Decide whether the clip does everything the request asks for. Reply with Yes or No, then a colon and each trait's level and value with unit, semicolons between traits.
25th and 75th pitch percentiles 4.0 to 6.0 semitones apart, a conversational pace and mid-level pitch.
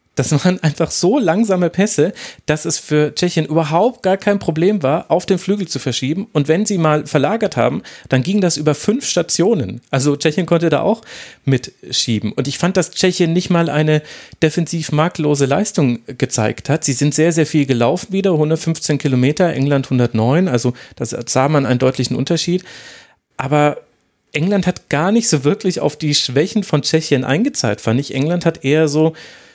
Yes: average, 4.3 semitones; average, 180 wpm; medium, 155 Hz